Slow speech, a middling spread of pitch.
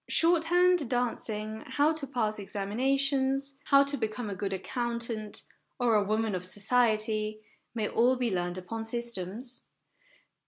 Yes: slow, 130 wpm; average, 4.0 semitones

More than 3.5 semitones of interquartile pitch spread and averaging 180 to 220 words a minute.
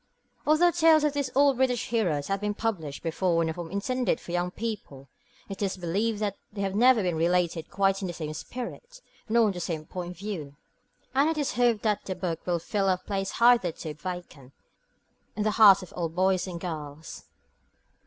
Yes: average, 5.0 semitones; average, 200 wpm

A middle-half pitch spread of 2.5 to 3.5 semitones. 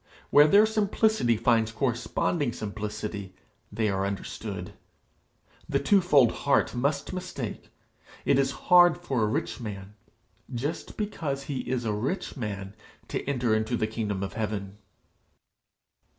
No: average, 5.2 semitones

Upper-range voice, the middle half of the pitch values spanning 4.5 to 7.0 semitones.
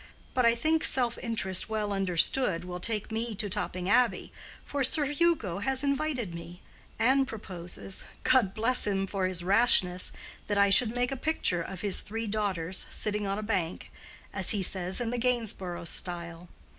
Yes: high, 205 Hz; average, 4.8 semitones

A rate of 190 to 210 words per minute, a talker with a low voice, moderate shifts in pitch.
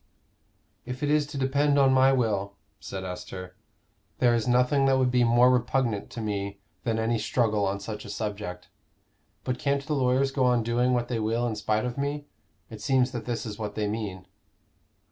Yes: average, 195 wpm; low, 120 Hz; average, 3.8 semitones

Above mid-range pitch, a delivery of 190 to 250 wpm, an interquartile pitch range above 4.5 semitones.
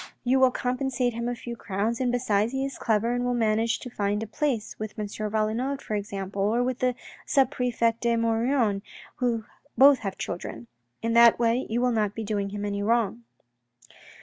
No: high, 230 Hz; average, 200 wpm; average, 2.7 semitones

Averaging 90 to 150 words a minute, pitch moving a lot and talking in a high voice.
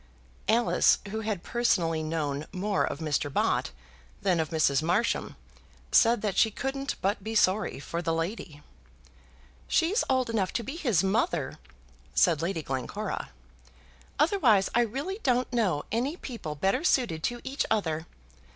Yes: average, 145 wpm; wide, 6.6 semitones; high, 205 Hz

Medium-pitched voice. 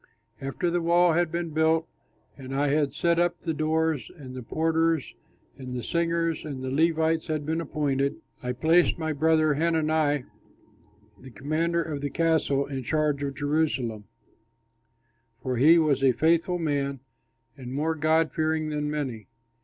Yes: medium, 155 Hz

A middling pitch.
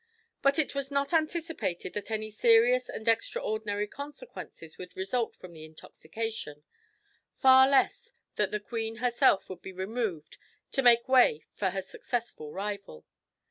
No: high, 225 Hz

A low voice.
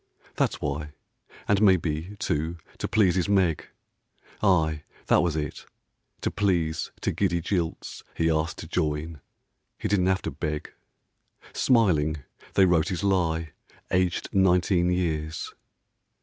Yes: very low, 85 Hz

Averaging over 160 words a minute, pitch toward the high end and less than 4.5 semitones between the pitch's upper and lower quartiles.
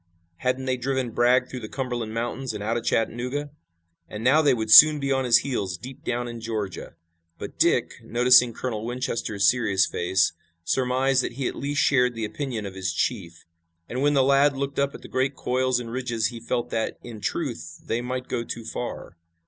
No: average, 200 wpm; low, 125 Hz; average, 2.9 semitones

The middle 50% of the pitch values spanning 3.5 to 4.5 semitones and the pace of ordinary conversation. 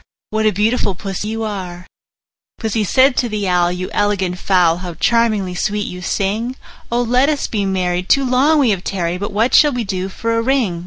No: average, 4.2 semitones; fast, 210 wpm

